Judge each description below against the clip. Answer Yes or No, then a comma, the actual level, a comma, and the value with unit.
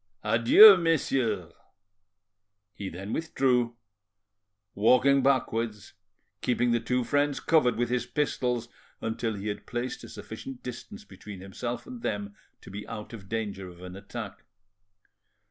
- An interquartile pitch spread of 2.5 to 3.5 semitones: No, average, 4.0 semitones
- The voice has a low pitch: Yes, low, 120 Hz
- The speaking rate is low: Yes, slow, 130 wpm